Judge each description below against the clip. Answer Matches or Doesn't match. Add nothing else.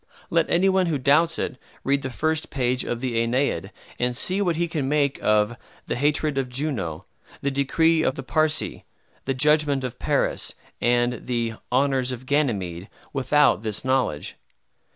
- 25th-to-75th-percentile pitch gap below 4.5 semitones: Matches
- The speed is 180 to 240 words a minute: Doesn't match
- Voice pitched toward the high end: Doesn't match